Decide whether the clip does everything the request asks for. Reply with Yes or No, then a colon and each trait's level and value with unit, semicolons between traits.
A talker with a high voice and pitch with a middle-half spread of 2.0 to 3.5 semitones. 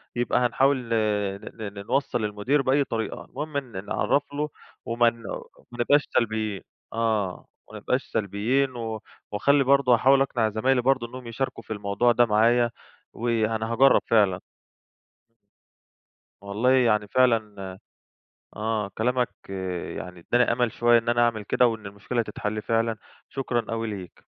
No: low, 115 Hz; average, 2.8 semitones